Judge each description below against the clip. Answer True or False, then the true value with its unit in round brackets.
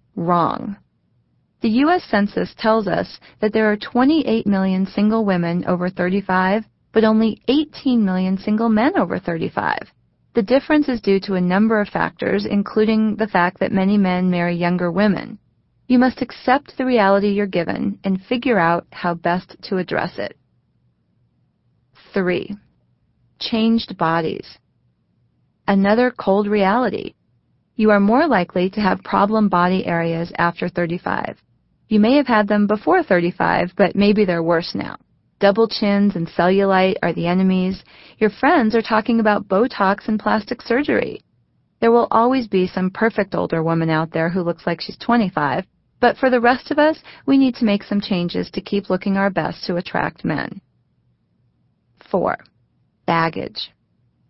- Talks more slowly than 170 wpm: True (150 wpm)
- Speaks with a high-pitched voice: True (205 Hz)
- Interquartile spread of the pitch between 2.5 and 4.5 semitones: True (3.9 semitones)